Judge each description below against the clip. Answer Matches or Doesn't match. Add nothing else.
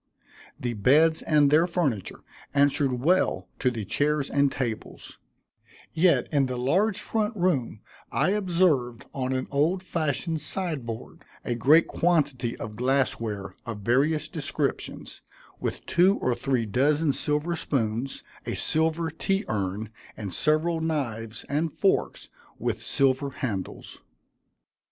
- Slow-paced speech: Matches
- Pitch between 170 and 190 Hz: Doesn't match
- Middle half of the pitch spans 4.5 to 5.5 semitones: Matches